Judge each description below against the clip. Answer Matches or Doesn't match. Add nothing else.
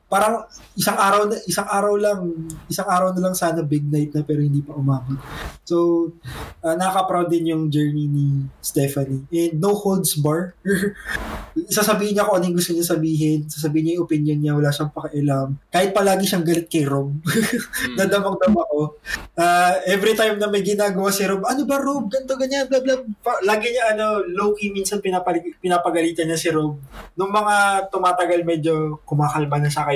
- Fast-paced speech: Matches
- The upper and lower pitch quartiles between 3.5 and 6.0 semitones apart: Matches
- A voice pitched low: Doesn't match